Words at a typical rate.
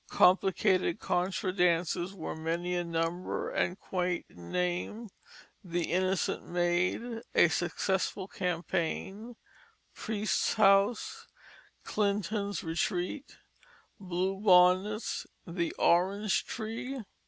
No: slow, 90 wpm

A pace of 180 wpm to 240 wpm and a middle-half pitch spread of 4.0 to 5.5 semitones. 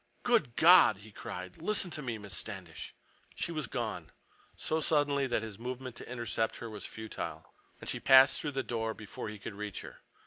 Yes: average, 185 wpm; average, 5.2 semitones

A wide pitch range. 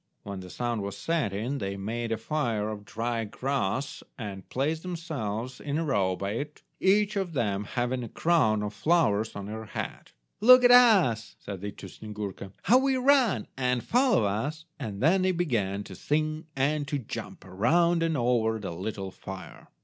Yes: wide, 7.6 semitones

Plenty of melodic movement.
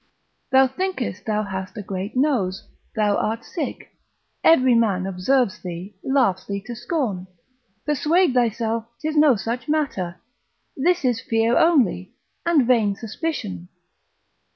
Yes: wide, 5.7 semitones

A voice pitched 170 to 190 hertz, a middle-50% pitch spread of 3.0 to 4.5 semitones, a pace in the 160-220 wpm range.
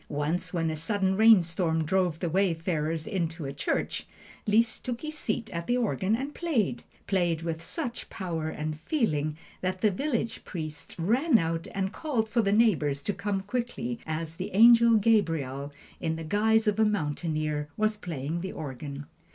No: medium, 185 Hz; wide, 5.6 semitones; average, 165 wpm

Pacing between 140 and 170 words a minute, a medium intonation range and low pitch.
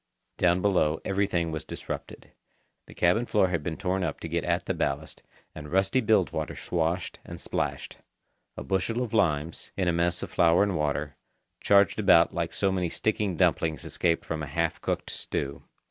No: average, 180 wpm; average, 3.5 semitones; very low, 85 Hz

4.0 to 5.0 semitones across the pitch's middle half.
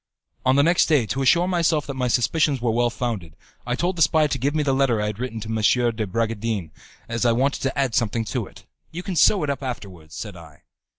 Yes: average, 4.4 semitones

